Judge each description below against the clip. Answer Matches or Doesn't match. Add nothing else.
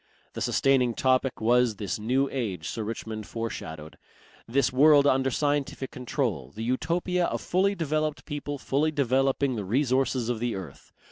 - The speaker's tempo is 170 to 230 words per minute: Doesn't match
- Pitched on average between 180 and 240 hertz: Doesn't match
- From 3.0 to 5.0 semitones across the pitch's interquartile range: Matches